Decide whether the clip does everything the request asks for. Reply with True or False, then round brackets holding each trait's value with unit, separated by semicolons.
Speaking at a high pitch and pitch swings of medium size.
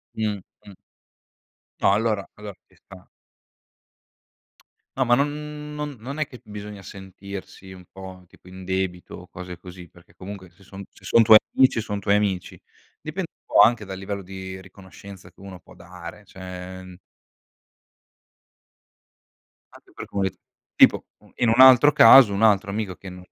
False (100 Hz; 3.2 semitones)